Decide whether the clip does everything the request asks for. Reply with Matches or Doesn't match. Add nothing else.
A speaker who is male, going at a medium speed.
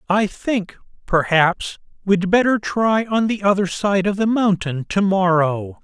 Matches